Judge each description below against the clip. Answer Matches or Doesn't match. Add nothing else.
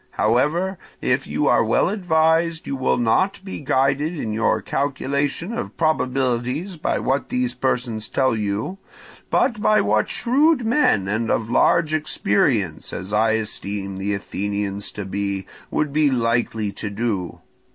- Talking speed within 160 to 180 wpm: Doesn't match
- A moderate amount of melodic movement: Doesn't match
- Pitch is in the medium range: Doesn't match